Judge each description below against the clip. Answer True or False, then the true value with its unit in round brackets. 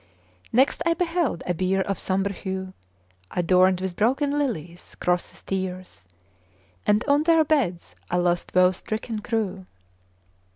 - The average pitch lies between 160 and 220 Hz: True (190 Hz)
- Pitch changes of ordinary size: False (6.2 semitones)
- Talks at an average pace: False (130 wpm)